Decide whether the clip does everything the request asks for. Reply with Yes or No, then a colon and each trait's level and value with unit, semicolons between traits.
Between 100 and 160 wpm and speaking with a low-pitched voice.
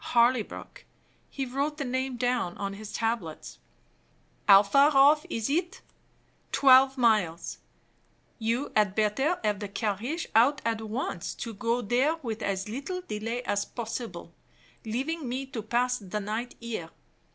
No: average, 140 wpm; high, 235 Hz